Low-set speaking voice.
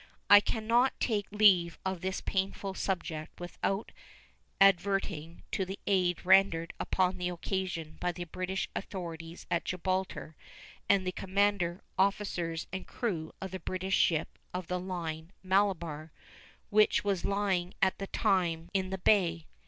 No: medium, 185 Hz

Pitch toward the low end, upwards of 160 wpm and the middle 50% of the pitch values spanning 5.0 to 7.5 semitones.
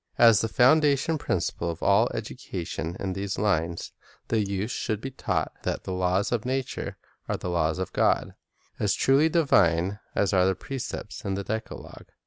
Yes: low, 100 Hz; average, 175 wpm; average, 5.3 semitones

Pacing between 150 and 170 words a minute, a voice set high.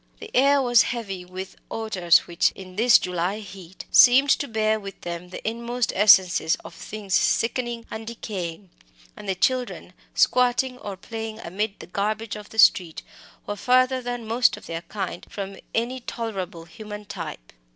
Yes: average, 160 wpm; high, 215 Hz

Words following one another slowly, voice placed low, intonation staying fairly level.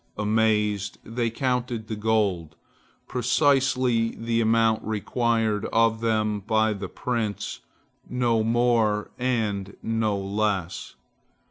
Yes: slow, 100 wpm; low, 110 Hz; narrow, 1.9 semitones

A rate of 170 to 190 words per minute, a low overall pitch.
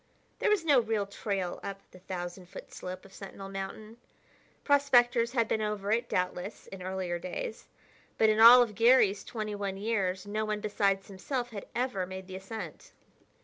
No: average, 175 wpm; high, 205 Hz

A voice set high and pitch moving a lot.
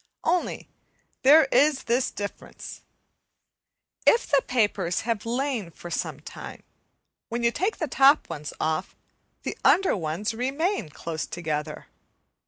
Yes: high, 235 Hz; wide, 8.4 semitones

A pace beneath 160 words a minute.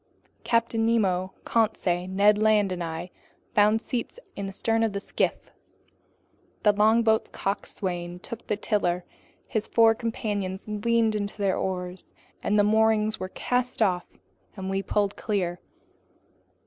Yes: slow, 135 wpm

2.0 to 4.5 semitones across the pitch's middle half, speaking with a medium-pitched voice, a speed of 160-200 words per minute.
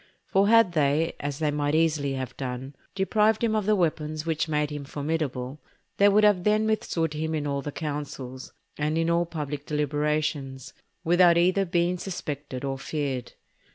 Yes: average, 3.5 semitones; medium, 155 Hz; average, 170 wpm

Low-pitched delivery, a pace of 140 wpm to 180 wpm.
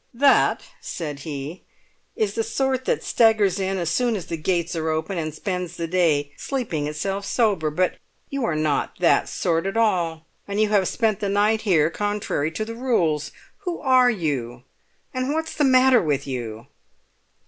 No: high, 190 Hz; average, 175 wpm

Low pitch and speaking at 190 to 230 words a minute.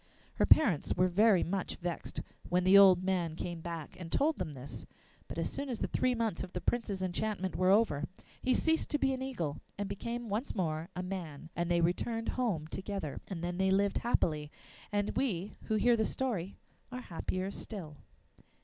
No: high, 190 Hz; average, 195 wpm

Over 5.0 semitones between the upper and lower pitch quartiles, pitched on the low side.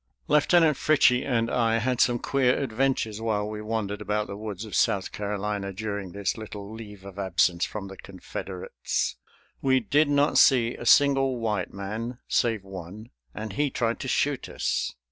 No: average, 3.8 semitones; low, 110 Hz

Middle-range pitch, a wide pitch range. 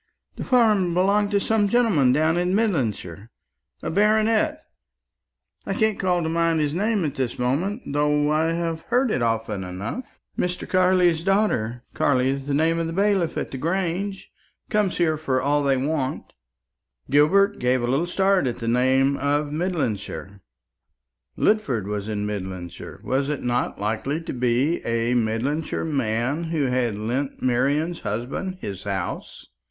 Yes: medium, 150 Hz; wide, 6.8 semitones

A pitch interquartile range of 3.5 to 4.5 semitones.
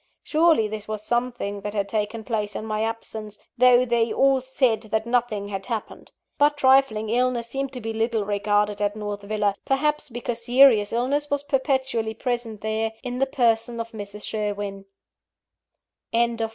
No: average, 3.0 semitones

